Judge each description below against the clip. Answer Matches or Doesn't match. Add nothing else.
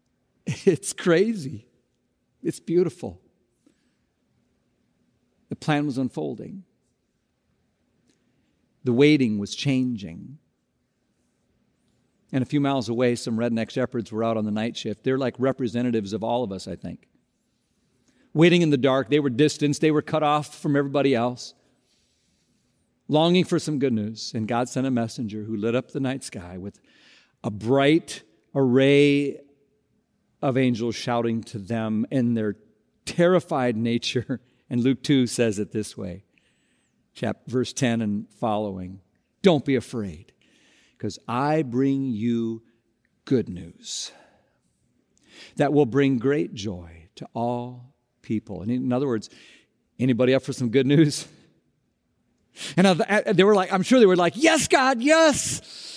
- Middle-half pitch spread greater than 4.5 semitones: Doesn't match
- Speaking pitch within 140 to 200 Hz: Doesn't match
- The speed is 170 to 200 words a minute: Doesn't match